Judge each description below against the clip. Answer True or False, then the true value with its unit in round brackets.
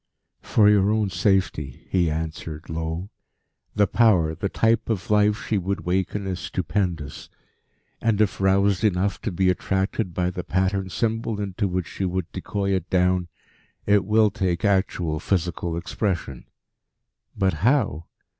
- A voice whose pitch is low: True (95 Hz)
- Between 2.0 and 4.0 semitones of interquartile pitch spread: True (2.9 semitones)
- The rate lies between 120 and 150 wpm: True (145 wpm)